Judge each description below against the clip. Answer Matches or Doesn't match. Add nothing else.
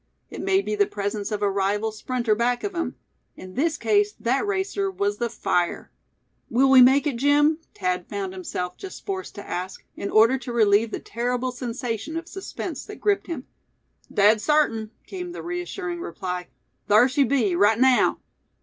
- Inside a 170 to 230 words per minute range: Matches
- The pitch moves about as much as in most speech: Doesn't match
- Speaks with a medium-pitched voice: Doesn't match